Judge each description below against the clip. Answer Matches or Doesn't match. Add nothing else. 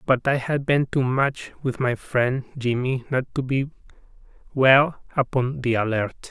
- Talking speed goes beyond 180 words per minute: Doesn't match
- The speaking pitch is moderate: Doesn't match